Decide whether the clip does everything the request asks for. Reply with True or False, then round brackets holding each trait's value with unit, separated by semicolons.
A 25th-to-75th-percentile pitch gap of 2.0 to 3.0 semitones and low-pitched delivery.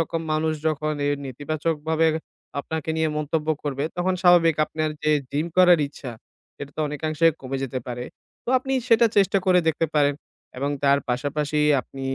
False (2.5 semitones; 155 Hz)